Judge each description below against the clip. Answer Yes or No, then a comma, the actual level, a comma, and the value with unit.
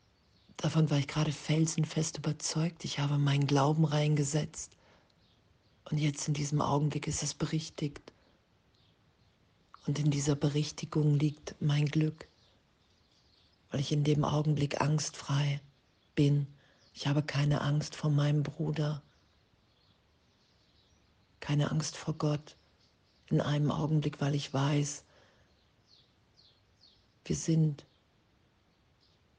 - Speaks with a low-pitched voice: No, medium, 145 Hz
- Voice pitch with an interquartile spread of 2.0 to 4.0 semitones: Yes, average, 3.1 semitones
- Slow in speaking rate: Yes, slow, 105 wpm